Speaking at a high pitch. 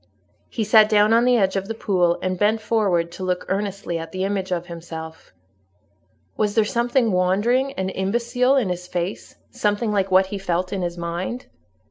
Yes: high, 195 Hz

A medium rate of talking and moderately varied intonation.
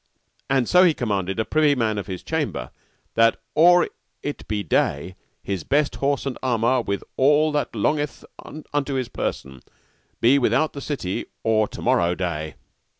No: average, 160 wpm; wide, 6.7 semitones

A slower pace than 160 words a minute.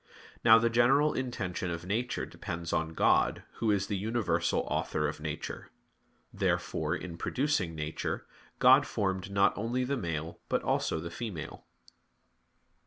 Yes: average, 140 wpm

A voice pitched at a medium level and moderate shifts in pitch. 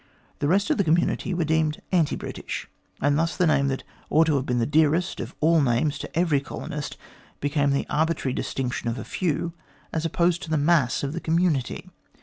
Yes: medium, 155 Hz; average, 3.0 semitones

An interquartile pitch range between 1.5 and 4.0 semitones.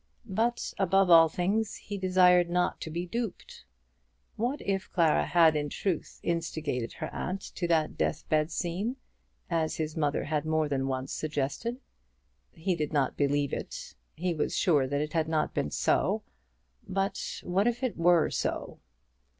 Yes: average, 3.7 semitones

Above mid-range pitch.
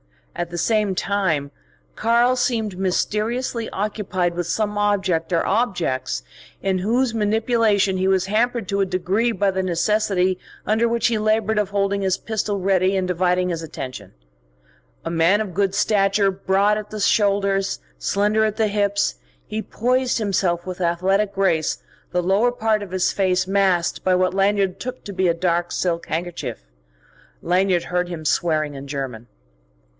Yes: high, 195 Hz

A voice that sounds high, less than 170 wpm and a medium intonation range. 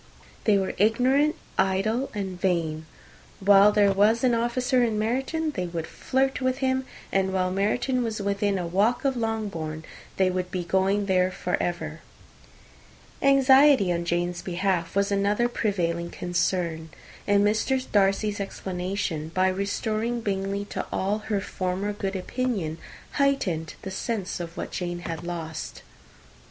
Yes: high, 195 Hz; average, 145 wpm; average, 4.1 semitones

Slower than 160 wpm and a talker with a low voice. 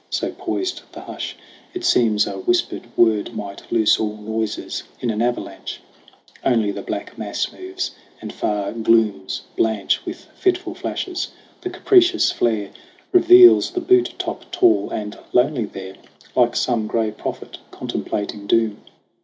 Yes: average, 140 wpm; low, 115 Hz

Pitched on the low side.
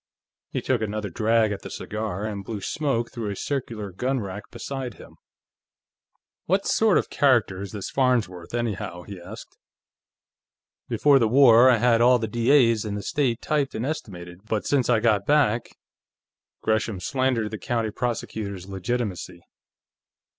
Yes: low, 115 Hz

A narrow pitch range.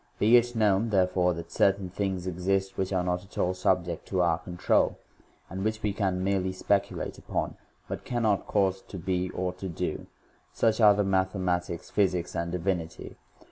Yes: narrow, 1.8 semitones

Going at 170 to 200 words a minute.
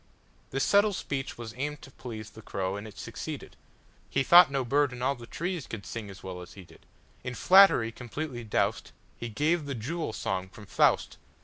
Yes: average, 175 wpm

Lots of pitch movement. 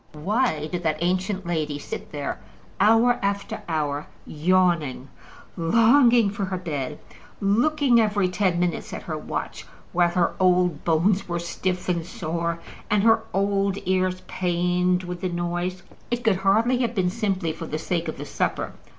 No: average, 3.0 semitones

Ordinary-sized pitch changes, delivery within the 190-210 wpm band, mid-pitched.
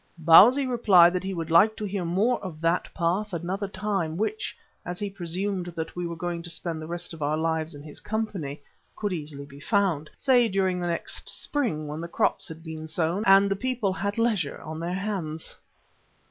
Yes: average, 3.9 semitones; average, 200 wpm; medium, 175 Hz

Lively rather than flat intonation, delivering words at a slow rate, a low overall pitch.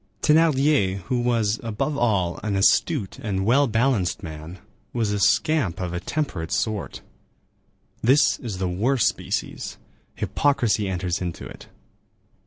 Yes: wide, 6.0 semitones; slow, 130 wpm; low, 105 Hz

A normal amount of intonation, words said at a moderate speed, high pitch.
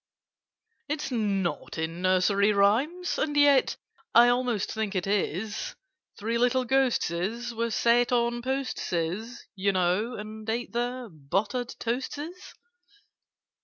No: average, 3.9 semitones; slow, 115 wpm; high, 230 Hz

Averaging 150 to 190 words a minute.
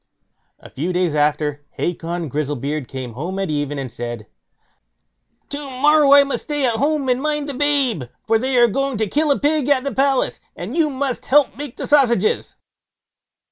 Yes: average, 185 wpm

